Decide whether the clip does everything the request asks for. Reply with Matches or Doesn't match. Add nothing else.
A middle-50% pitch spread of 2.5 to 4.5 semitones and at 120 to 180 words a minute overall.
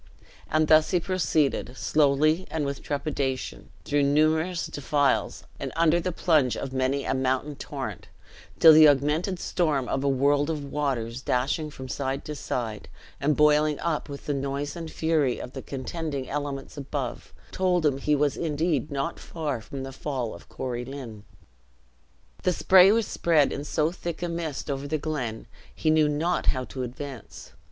Matches